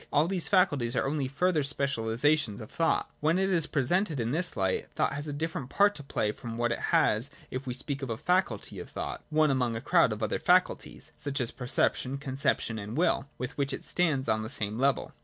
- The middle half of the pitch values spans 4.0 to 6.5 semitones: Yes, average, 4.5 semitones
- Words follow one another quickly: Yes, fast, 220 wpm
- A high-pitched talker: No, medium, 140 Hz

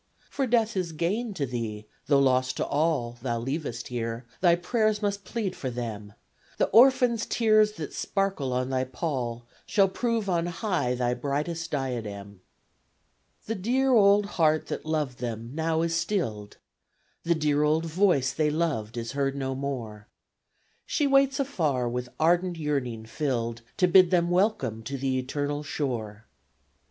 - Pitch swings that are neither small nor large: No, wide, 7.1 semitones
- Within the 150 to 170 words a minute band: Yes, average, 155 wpm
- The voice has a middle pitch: Yes, medium, 150 Hz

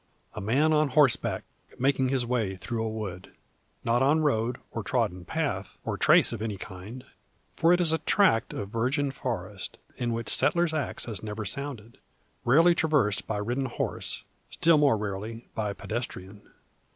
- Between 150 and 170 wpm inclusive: Yes, average, 165 wpm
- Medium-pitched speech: No, low, 120 Hz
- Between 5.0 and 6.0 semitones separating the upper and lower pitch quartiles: Yes, average, 5.3 semitones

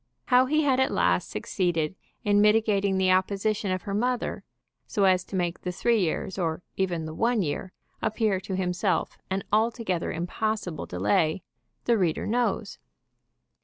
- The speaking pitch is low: No, high, 195 Hz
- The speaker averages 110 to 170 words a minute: Yes, average, 155 wpm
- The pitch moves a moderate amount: Yes, average, 3.6 semitones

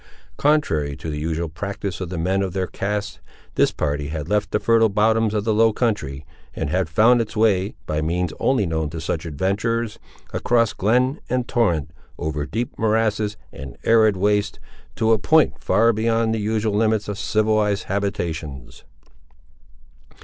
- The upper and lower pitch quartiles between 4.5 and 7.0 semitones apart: Yes, average, 5.2 semitones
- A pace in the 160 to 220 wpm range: Yes, average, 165 wpm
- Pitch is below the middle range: Yes, low, 105 Hz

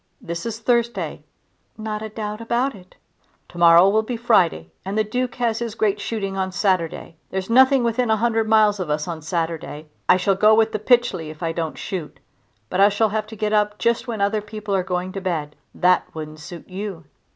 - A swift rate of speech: Yes, fast, 210 wpm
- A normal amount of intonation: Yes, average, 3.8 semitones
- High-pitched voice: Yes, high, 205 Hz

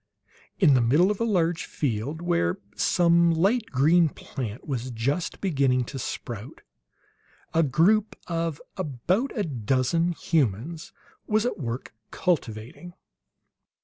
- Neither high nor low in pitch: Yes, medium, 160 Hz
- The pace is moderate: No, slow, 120 wpm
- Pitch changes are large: Yes, wide, 5.7 semitones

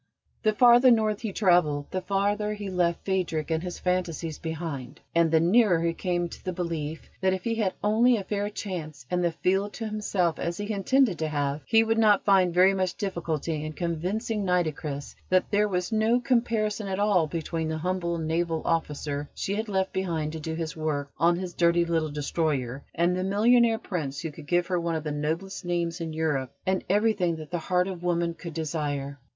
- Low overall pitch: No, medium, 175 Hz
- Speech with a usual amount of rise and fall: Yes, average, 3.9 semitones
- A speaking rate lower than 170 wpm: No, average, 200 wpm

